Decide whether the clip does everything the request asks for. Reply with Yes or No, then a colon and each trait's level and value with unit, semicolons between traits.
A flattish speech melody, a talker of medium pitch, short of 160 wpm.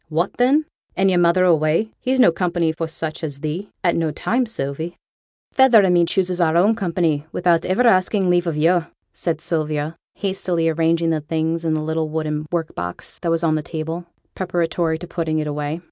No: narrow, 2.3 semitones; medium, 165 Hz; average, 195 wpm